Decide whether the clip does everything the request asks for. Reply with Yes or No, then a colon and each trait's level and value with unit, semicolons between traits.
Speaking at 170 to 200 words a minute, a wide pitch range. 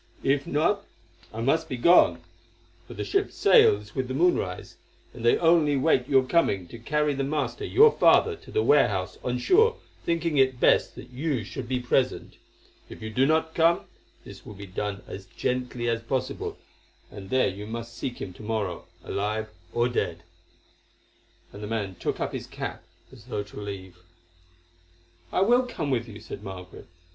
Yes: average, 175 wpm; wide, 6.4 semitones